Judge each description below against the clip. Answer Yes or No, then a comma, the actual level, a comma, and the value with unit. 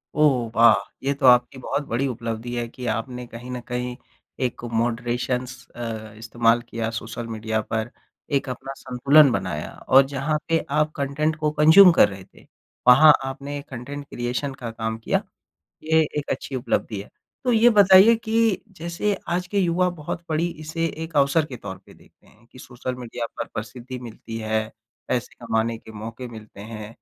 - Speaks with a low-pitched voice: Yes, low, 125 Hz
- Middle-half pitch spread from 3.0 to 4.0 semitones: No, average, 4.8 semitones